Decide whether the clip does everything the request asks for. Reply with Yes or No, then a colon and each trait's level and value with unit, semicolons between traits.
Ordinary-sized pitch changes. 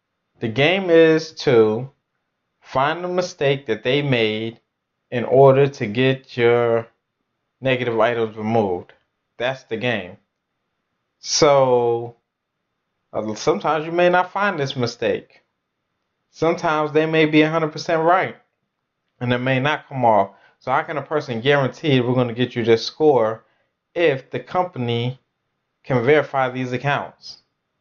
Yes: average, 4.5 semitones